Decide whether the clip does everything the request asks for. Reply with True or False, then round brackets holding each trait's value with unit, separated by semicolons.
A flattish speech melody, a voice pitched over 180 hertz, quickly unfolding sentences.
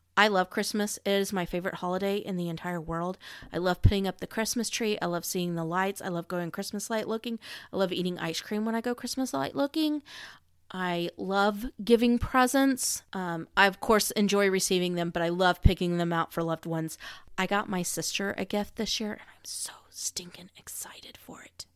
False (3.6 semitones; 190 Hz; 210 wpm)